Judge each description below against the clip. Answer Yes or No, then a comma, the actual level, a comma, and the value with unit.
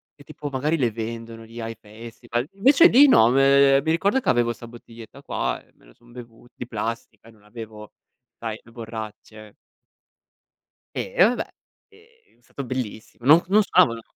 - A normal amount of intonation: Yes, average, 3.7 semitones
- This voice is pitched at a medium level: No, low, 120 Hz